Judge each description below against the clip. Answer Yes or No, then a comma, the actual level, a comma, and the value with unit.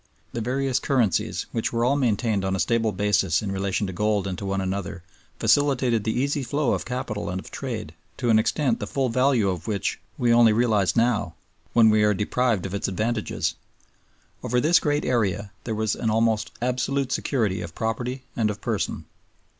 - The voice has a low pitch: Yes, low, 110 Hz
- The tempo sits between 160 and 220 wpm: Yes, average, 190 wpm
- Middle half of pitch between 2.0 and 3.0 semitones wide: No, average, 3.7 semitones